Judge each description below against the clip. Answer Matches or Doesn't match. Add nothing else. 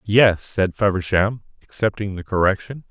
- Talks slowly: Matches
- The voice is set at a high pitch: Doesn't match